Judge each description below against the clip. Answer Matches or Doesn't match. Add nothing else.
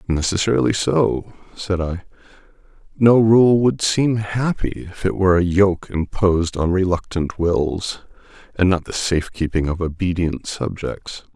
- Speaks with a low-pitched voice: Matches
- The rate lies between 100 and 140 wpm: Matches